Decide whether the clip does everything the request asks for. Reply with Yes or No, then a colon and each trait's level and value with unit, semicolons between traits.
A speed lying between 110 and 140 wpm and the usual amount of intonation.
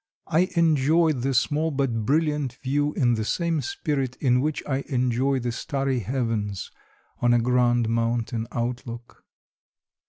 Yes: slow, 135 wpm; average, 3.5 semitones